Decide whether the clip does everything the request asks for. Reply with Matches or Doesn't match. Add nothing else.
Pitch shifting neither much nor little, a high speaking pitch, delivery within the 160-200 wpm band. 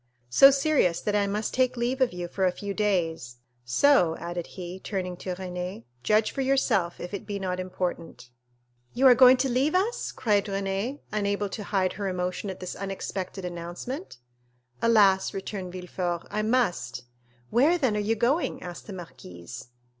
Matches